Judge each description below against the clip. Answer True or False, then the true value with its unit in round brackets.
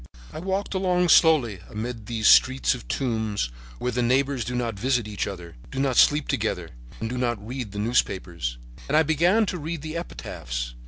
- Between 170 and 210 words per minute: True (190 wpm)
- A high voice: False (125 Hz)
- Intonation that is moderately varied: False (6.2 semitones)